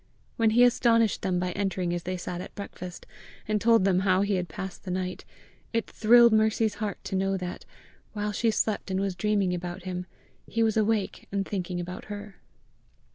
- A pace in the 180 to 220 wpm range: Yes, average, 190 wpm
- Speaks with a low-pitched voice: No, high, 195 Hz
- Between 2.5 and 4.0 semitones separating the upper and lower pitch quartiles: Yes, average, 3.0 semitones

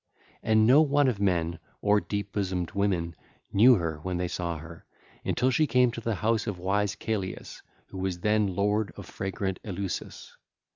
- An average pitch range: Yes, average, 3.4 semitones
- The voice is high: No, low, 100 Hz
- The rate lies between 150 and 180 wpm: Yes, average, 175 wpm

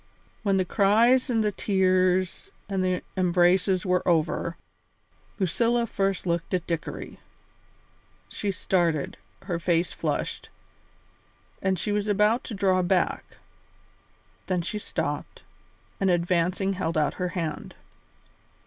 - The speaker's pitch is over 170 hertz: Yes, medium, 185 Hz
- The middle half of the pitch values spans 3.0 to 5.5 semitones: No, narrow, 2.4 semitones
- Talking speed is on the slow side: Yes, slow, 120 wpm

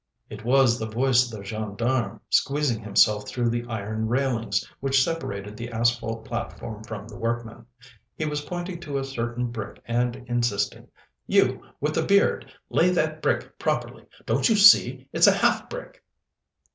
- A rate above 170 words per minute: No, average, 160 wpm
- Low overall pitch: Yes, low, 120 Hz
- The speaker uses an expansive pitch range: No, average, 3.5 semitones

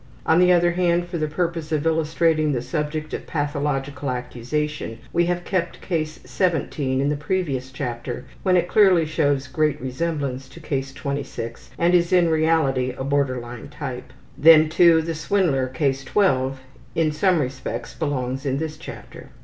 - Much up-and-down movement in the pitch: No, average, 3.9 semitones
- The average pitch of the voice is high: No, medium, 150 Hz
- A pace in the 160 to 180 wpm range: Yes, average, 165 wpm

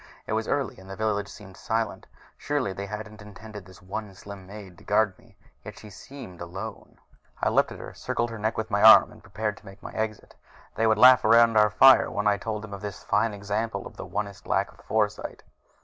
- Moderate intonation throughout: No, narrow, 1.9 semitones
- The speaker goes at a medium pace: No, fast, 220 wpm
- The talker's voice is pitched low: Yes, low, 105 Hz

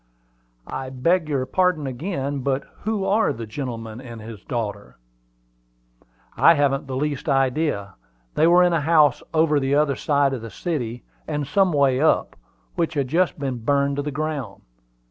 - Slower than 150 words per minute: No, average, 165 wpm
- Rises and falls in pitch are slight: No, average, 3.5 semitones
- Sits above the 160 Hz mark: No, medium, 140 Hz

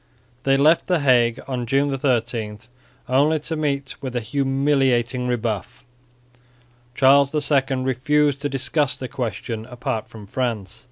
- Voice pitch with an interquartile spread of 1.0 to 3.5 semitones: Yes, average, 2.8 semitones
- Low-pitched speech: Yes, low, 130 Hz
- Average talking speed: No, slow, 130 wpm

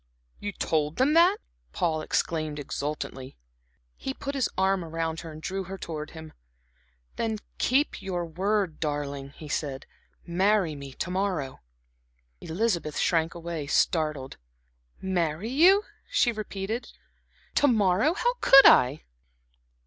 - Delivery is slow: Yes, slow, 125 wpm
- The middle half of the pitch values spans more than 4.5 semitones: Yes, wide, 5.5 semitones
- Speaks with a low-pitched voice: No, medium, 170 Hz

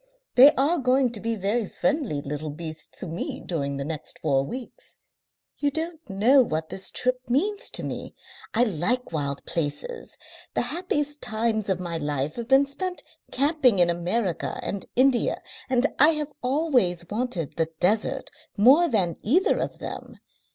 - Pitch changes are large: Yes, wide, 8.2 semitones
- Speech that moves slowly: No, average, 160 wpm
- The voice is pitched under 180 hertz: No, high, 230 Hz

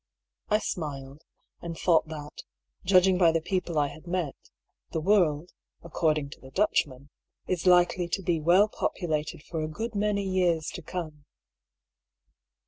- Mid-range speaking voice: Yes, medium, 170 Hz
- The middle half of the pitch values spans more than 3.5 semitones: No, average, 3.2 semitones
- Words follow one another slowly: No, average, 145 wpm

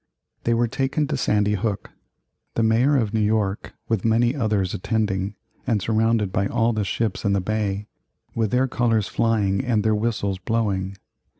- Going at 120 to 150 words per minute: No, average, 170 wpm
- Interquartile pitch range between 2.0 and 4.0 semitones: Yes, narrow, 2.4 semitones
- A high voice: No, low, 110 Hz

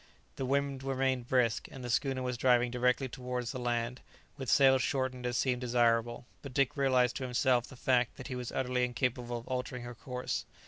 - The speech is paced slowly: No, average, 195 wpm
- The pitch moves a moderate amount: No, narrow, 1.3 semitones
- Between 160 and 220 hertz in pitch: No, low, 125 Hz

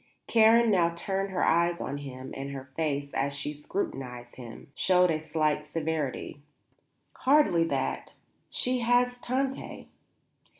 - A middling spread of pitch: No, wide, 6.6 semitones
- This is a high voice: No, medium, 160 Hz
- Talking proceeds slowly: Yes, slow, 130 wpm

